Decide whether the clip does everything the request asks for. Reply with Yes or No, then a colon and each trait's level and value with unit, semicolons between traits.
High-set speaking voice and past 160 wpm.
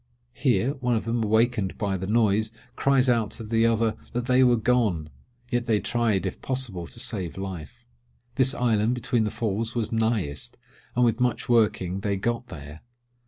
No: low, 115 Hz; average, 170 wpm